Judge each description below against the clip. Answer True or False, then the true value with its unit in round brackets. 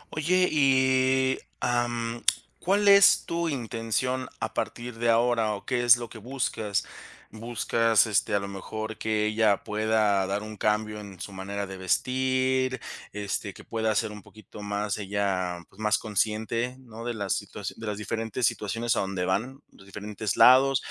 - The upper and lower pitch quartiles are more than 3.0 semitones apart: True (3.4 semitones)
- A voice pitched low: True (110 Hz)